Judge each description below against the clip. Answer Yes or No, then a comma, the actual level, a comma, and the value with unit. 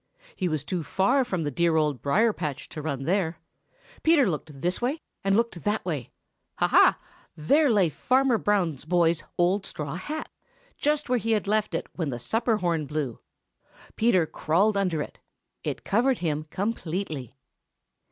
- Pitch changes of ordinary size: No, wide, 6.1 semitones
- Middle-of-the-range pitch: Yes, medium, 180 Hz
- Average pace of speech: Yes, average, 165 wpm